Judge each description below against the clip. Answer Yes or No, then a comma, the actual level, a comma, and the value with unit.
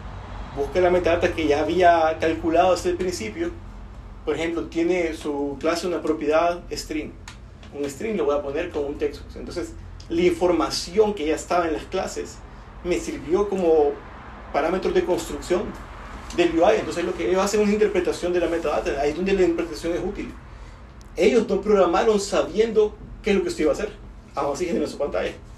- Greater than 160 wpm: Yes, average, 185 wpm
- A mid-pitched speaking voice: Yes, medium, 170 Hz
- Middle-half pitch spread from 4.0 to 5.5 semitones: No, average, 3.6 semitones